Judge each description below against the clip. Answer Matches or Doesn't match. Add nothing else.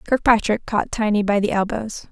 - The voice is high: Matches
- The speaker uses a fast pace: Doesn't match